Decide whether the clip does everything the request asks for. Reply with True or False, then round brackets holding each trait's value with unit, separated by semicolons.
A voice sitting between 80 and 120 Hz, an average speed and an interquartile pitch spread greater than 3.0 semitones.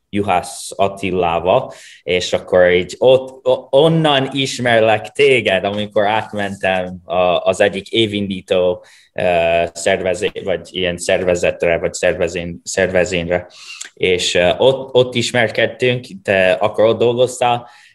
False (100 Hz; 95 wpm; 5.5 semitones)